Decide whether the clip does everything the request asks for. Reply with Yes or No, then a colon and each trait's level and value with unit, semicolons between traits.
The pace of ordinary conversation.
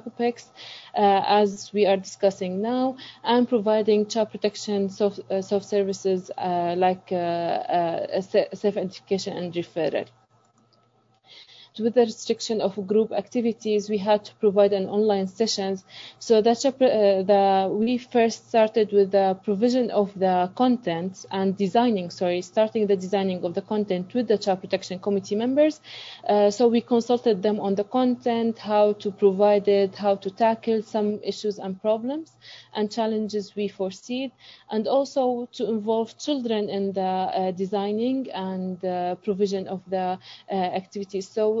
Yes: average, 145 wpm